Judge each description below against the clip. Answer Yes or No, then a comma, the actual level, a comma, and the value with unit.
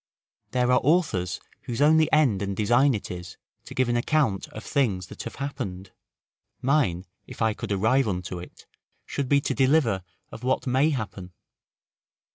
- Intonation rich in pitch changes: Yes, wide, 6.2 semitones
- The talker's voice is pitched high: No, low, 120 Hz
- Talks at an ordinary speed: Yes, average, 165 wpm